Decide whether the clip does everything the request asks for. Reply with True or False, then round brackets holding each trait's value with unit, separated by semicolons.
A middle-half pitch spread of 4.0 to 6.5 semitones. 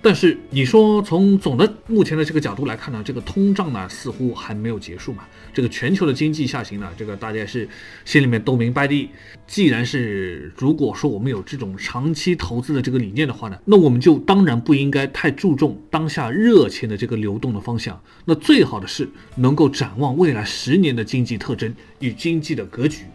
True (5.6 semitones)